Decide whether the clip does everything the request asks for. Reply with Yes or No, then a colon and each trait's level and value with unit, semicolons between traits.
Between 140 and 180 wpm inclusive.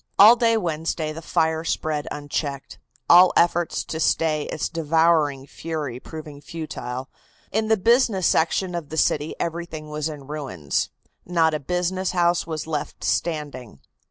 Yes: average, 145 wpm